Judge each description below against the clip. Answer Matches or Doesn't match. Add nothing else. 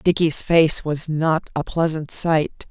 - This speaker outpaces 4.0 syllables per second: Doesn't match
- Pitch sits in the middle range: Matches